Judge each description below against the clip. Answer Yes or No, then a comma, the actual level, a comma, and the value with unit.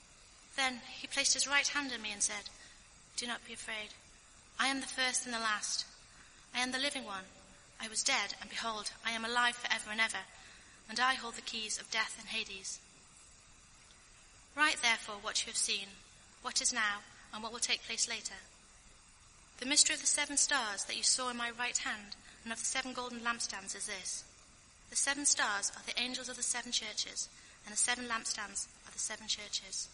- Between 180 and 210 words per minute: Yes, average, 200 wpm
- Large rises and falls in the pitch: No, average, 3.0 semitones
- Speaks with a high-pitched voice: Yes, high, 235 Hz